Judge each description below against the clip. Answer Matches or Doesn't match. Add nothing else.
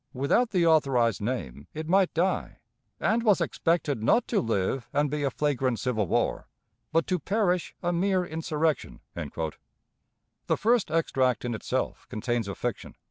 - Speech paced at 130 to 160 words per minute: Matches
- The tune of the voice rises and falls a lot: Matches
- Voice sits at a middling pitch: Matches